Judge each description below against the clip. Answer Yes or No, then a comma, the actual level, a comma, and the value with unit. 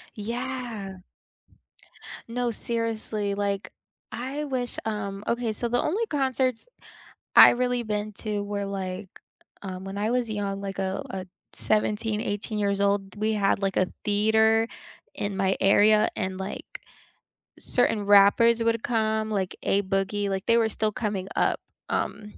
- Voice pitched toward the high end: Yes, high, 210 Hz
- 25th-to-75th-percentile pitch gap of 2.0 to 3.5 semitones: Yes, narrow, 2.5 semitones